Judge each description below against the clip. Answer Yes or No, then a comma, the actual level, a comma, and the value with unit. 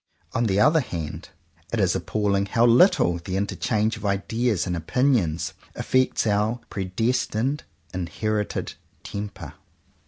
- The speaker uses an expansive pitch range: No, average, 3.8 semitones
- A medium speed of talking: No, slow, 120 wpm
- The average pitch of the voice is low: Yes, low, 105 Hz